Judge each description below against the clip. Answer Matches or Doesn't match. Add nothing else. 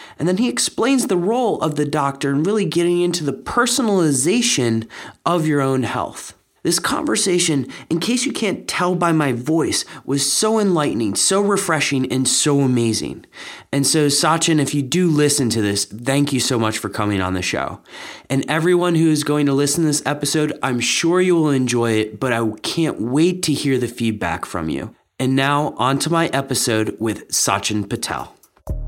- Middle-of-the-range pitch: Matches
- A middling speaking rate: Matches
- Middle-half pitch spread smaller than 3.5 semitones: Doesn't match